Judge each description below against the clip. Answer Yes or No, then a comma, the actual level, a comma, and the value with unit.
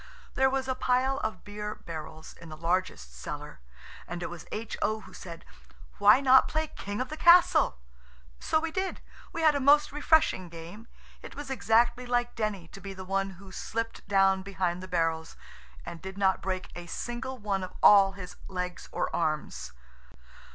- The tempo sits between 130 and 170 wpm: No, average, 180 wpm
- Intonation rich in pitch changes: Yes, wide, 6.1 semitones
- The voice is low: No, high, 200 Hz